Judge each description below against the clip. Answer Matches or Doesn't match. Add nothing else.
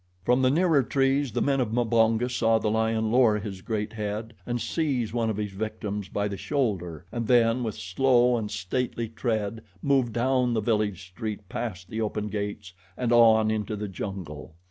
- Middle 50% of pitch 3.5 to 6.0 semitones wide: Doesn't match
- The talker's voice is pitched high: Doesn't match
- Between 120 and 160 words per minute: Doesn't match